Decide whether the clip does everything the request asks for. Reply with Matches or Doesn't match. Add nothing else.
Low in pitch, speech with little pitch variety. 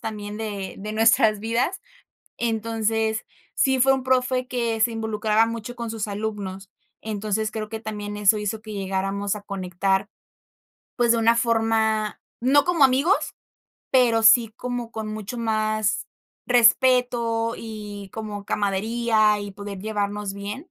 Doesn't match